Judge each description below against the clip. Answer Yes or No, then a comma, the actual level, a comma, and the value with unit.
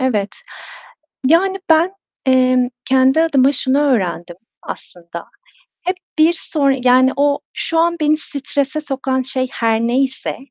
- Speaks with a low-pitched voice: No, very high, 265 Hz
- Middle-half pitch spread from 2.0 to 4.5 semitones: Yes, average, 3.2 semitones